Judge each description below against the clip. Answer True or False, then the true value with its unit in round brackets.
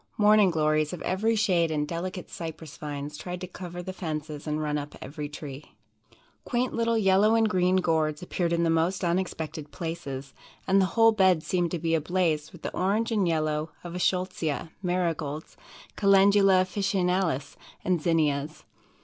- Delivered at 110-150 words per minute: False (165 wpm)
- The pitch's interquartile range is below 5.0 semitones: True (3.5 semitones)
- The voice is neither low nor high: True (175 Hz)